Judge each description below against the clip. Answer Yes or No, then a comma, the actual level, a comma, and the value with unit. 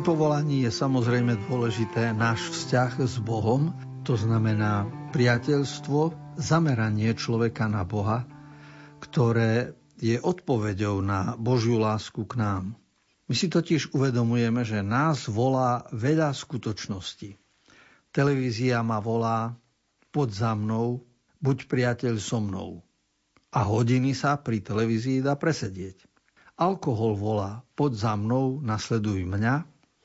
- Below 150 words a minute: Yes, slow, 110 wpm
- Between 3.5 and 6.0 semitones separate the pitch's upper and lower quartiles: Yes, average, 4.0 semitones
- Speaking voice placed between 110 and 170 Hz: Yes, low, 120 Hz